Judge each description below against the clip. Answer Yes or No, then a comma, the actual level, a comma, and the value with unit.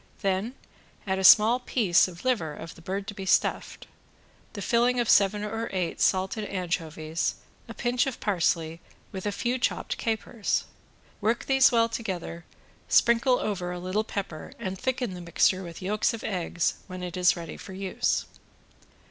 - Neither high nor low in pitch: No, high, 195 Hz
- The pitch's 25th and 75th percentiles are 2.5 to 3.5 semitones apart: No, average, 4.3 semitones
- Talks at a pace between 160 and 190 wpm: Yes, average, 165 wpm